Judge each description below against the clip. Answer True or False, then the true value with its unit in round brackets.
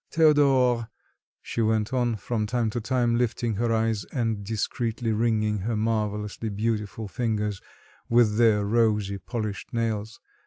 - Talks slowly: True (130 wpm)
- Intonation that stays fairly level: True (2.0 semitones)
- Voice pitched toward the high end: False (110 Hz)